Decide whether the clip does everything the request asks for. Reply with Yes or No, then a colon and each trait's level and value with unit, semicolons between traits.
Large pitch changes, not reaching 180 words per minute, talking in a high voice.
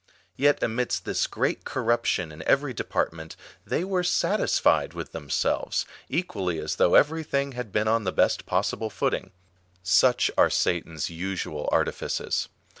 No: wide, 7.7 semitones; average, 150 wpm; low, 110 Hz